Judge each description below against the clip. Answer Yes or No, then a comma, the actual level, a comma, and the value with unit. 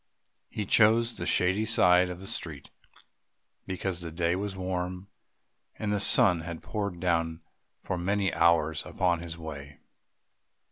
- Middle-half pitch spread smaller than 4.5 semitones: Yes, average, 2.7 semitones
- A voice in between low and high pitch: No, very low, 90 Hz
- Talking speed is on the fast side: No, average, 140 wpm